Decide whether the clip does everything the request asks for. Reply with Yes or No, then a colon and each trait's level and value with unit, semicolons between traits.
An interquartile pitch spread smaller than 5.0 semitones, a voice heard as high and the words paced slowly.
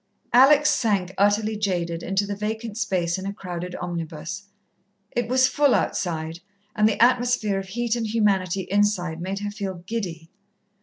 No: average, 3.6 semitones; high, 200 Hz; average, 155 wpm